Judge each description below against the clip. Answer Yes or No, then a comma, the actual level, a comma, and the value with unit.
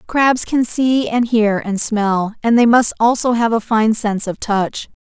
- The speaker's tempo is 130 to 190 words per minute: No, fast, 205 wpm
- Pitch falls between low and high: No, high, 225 Hz